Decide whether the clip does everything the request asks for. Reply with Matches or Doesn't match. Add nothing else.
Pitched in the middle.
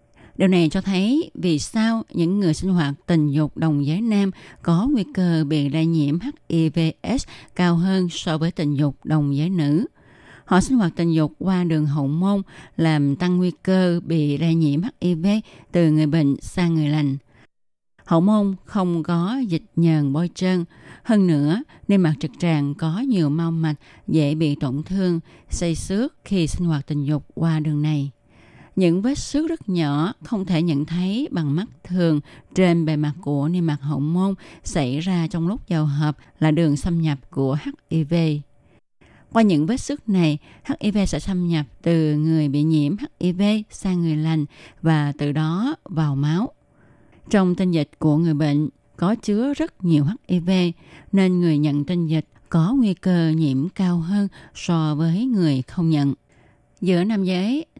Matches